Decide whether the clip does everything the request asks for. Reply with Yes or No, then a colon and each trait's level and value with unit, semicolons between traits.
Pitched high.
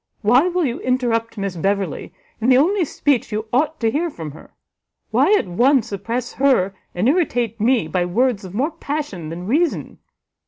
Yes: high, 240 Hz